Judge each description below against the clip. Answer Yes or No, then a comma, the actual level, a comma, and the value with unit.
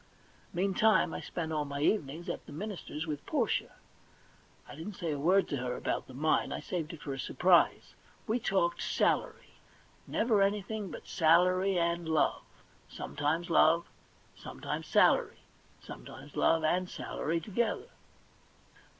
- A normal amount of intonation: Yes, average, 3.9 semitones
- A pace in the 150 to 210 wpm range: No, average, 140 wpm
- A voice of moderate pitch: Yes, medium, 170 Hz